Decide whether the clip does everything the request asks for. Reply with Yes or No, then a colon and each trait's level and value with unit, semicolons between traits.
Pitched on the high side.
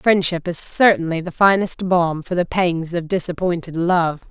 No: medium, 175 Hz